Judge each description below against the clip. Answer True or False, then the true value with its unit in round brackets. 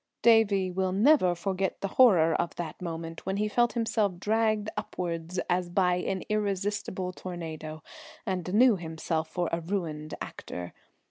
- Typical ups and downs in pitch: True (3.6 semitones)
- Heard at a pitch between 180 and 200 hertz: True (185 Hz)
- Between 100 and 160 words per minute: True (145 wpm)